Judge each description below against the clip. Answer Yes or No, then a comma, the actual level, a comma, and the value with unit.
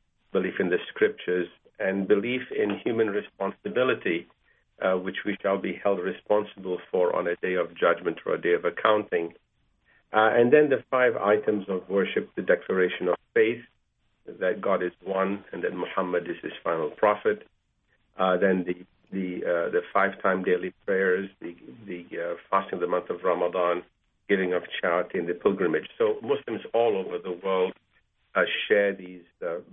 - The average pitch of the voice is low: Yes, low, 105 Hz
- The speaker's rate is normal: Yes, average, 170 wpm